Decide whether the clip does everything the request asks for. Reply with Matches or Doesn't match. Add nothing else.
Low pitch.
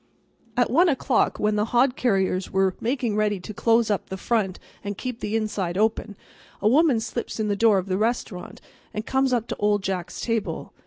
Doesn't match